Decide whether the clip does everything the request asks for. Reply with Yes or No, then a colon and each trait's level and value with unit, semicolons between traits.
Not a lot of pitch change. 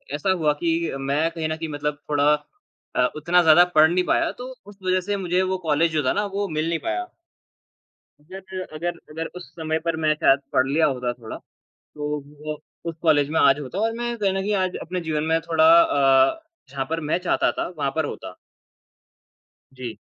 No: average, 3.7 semitones